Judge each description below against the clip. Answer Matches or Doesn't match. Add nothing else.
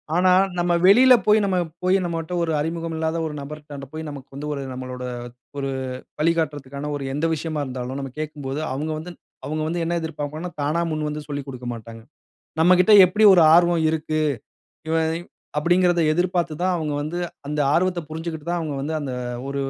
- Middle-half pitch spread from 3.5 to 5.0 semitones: Doesn't match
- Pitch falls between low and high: Matches